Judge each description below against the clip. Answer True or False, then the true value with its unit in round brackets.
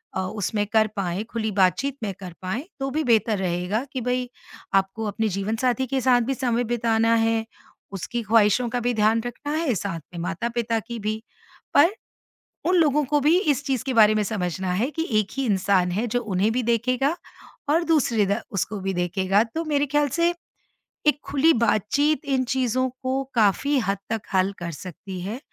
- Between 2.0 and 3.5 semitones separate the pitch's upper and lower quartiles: False (4.8 semitones)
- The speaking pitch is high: True (225 Hz)